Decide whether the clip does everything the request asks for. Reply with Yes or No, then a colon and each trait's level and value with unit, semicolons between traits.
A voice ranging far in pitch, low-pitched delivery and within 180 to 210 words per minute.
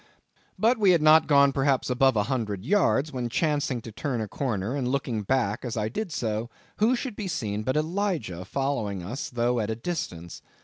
Yes: wide, 5.9 semitones; low, 130 Hz; average, 195 wpm